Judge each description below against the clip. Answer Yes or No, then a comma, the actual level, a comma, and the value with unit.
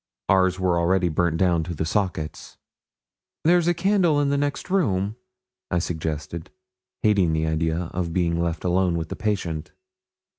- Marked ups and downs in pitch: No, average, 4.0 semitones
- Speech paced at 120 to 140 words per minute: No, average, 155 wpm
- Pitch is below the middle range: Yes, very low, 90 Hz